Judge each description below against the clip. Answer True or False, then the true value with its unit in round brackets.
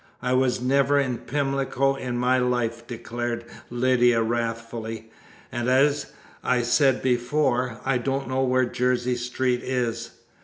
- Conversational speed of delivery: False (130 wpm)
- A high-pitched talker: False (125 Hz)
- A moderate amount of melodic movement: False (1.7 semitones)